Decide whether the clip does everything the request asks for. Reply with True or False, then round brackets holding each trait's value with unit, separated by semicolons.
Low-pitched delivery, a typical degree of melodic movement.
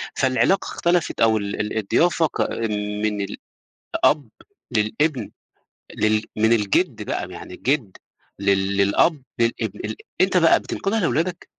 False (115 Hz; 6.9 semitones)